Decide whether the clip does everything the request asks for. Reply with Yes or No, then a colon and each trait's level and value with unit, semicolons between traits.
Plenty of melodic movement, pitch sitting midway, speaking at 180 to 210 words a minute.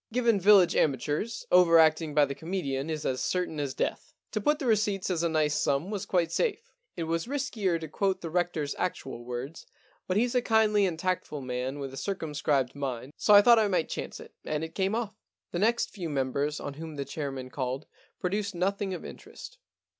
Yes: wide, 5.8 semitones; medium, 165 Hz; fast, 205 wpm